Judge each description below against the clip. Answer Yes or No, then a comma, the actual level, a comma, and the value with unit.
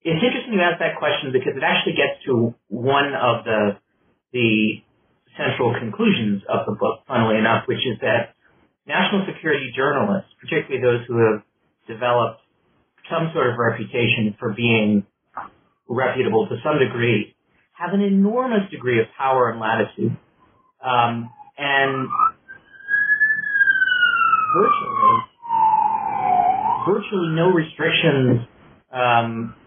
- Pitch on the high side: No, medium, 140 Hz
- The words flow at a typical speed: No, slow, 115 wpm